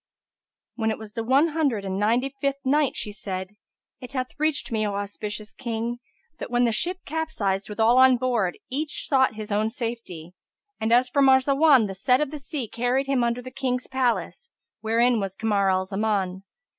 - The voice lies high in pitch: Yes, high, 235 Hz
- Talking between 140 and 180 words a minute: No, average, 190 wpm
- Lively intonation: No, average, 4.1 semitones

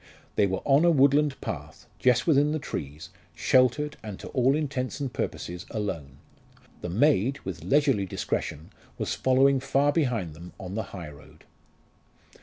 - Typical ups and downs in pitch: No, wide, 7.2 semitones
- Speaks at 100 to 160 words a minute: Yes, average, 155 wpm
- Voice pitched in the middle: No, low, 125 Hz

